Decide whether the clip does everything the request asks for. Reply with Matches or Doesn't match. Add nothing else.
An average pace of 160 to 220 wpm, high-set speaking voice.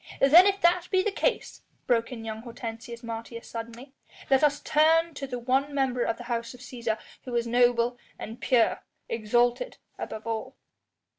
Matches